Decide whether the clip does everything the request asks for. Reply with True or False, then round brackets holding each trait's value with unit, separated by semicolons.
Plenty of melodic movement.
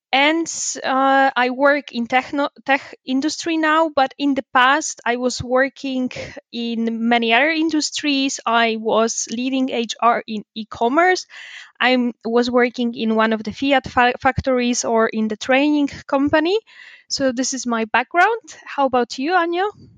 False (3.3 semitones)